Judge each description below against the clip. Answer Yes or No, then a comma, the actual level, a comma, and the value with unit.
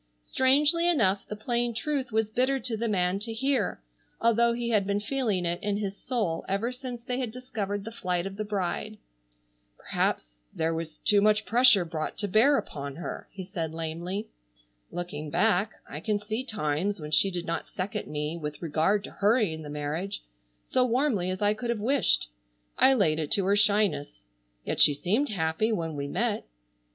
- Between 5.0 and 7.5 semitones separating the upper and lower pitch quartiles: Yes, wide, 5.5 semitones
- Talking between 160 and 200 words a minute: Yes, average, 185 wpm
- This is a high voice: Yes, high, 205 Hz